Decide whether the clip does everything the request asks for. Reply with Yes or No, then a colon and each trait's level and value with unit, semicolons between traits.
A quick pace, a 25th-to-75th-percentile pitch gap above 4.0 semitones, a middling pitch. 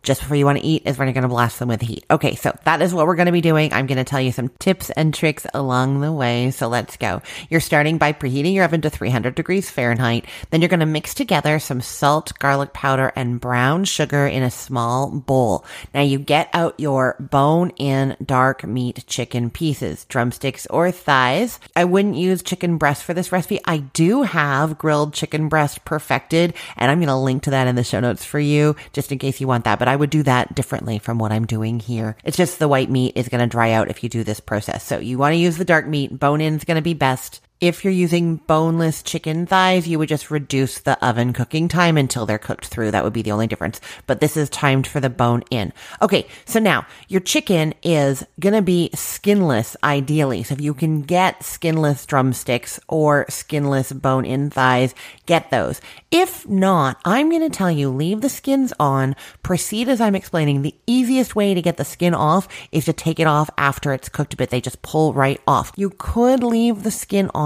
Yes: fast, 230 wpm; average, 4.5 semitones; medium, 145 Hz